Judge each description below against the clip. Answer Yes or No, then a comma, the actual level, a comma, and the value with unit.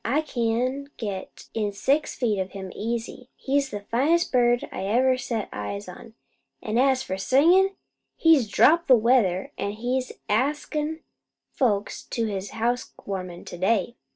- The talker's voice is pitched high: Yes, high, 235 Hz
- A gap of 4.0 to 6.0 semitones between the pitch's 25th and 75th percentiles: Yes, average, 4.8 semitones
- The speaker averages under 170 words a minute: Yes, average, 150 wpm